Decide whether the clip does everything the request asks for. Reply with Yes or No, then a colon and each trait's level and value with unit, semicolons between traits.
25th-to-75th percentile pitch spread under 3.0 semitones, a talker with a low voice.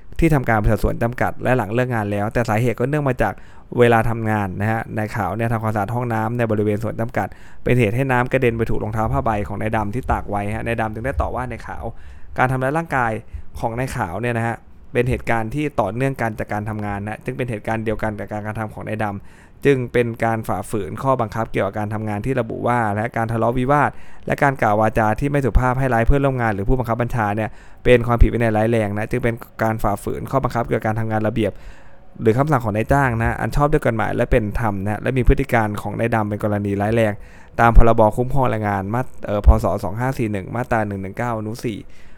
Yes: narrow, 2.5 semitones; low, 115 Hz